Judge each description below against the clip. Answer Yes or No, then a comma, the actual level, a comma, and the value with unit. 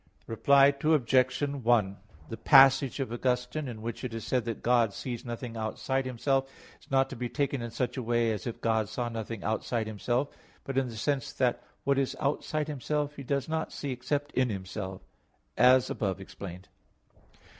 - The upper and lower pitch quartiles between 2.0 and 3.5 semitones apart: Yes, average, 3.1 semitones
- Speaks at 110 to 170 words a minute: No, average, 180 wpm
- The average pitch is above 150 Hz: No, low, 125 Hz